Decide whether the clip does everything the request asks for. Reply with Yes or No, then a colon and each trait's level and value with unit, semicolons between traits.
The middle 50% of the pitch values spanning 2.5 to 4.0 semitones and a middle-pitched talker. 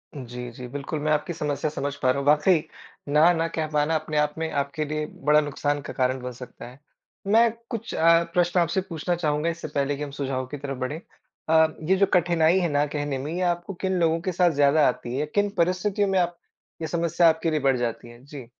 Yes: average, 3.4 semitones; medium, 150 Hz